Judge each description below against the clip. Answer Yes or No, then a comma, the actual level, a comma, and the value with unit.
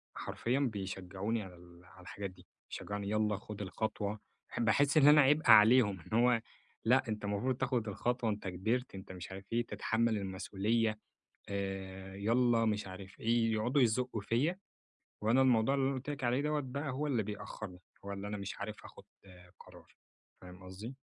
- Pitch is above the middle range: No, low, 110 Hz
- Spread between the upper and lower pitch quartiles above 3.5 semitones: Yes, average, 3.9 semitones